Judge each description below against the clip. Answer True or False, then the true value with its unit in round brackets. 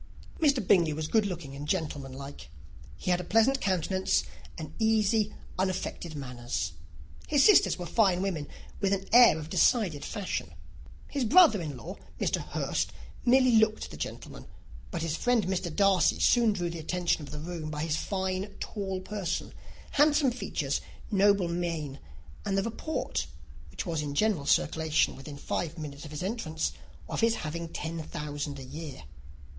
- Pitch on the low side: False (180 Hz)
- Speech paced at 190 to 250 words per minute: False (160 wpm)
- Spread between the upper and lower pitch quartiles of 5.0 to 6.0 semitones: True (5.4 semitones)